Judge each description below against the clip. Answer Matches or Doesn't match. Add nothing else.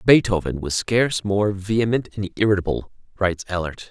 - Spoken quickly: Doesn't match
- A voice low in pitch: Matches